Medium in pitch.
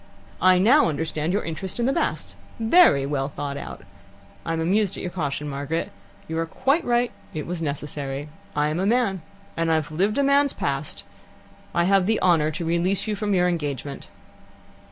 Yes: medium, 170 Hz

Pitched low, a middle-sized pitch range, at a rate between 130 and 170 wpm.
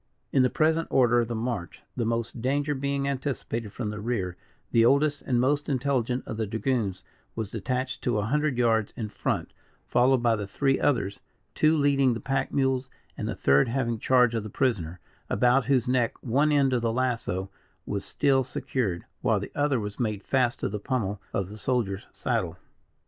No: low, 125 Hz; average, 3.7 semitones; average, 190 wpm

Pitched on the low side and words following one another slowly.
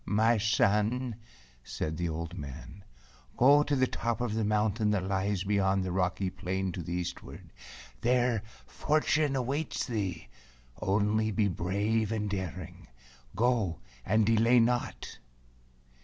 Yes: low, 105 Hz; slow, 130 wpm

